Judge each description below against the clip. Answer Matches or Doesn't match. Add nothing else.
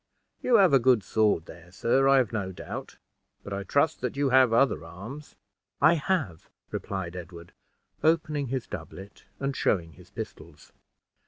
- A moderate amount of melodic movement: Doesn't match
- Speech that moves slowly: Doesn't match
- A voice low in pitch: Matches